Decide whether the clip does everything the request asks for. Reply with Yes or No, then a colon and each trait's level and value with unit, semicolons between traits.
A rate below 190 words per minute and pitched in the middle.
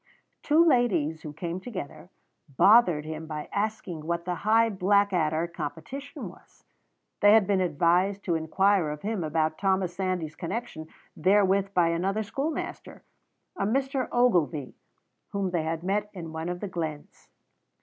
Yes: average, 145 wpm; medium, 180 Hz